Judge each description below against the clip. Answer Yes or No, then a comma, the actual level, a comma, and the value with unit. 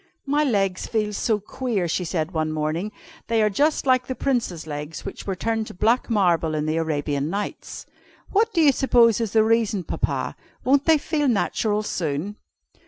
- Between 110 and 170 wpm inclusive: No, average, 180 wpm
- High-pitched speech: Yes, high, 210 Hz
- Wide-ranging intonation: Yes, wide, 7.0 semitones